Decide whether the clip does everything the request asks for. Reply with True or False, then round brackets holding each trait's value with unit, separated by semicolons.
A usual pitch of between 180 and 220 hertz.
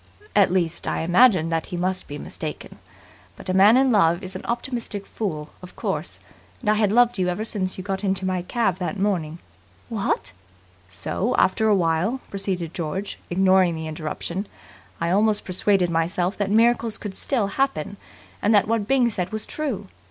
True (190 Hz)